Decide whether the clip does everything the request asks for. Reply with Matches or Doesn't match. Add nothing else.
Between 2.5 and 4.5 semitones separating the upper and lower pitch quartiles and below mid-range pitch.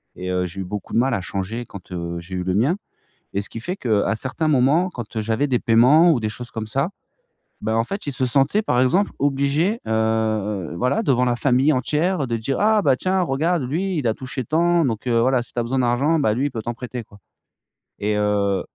Doesn't match